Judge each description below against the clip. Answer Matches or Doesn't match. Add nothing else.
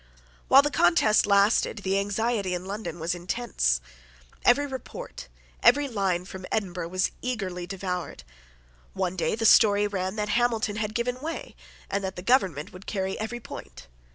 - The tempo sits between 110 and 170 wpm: Matches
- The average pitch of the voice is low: Doesn't match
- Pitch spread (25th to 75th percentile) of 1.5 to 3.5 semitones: Doesn't match